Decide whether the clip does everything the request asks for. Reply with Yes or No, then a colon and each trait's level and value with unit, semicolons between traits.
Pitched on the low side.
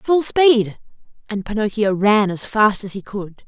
No: high, 215 Hz